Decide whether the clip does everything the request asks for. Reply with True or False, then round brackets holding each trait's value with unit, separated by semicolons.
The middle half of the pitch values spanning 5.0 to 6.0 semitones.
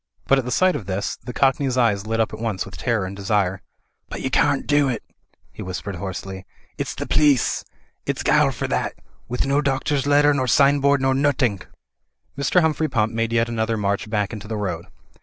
True (5.4 semitones)